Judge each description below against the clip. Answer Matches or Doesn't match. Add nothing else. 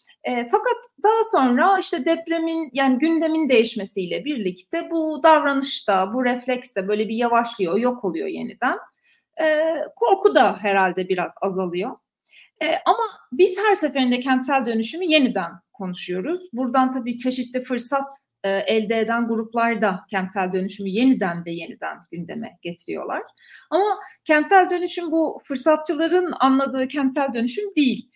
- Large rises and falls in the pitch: Matches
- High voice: Matches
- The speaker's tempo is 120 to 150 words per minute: Matches